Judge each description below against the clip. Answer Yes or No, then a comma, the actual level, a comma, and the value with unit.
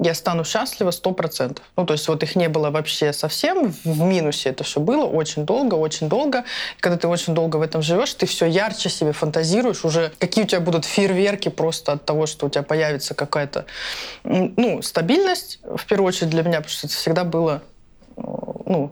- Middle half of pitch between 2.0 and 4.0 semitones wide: Yes, average, 3.2 semitones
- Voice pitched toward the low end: No, medium, 165 Hz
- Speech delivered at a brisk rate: Yes, fast, 200 wpm